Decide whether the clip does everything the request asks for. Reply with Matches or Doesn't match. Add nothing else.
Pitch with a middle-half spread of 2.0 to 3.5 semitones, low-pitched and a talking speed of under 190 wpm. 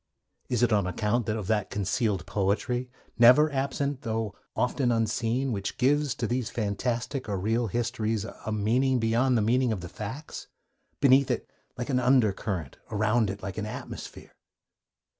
Matches